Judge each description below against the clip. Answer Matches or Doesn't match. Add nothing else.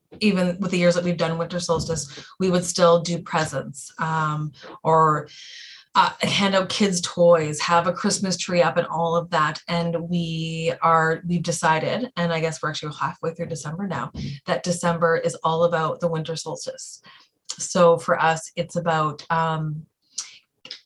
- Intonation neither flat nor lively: Doesn't match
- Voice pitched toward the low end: Doesn't match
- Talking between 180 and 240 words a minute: Doesn't match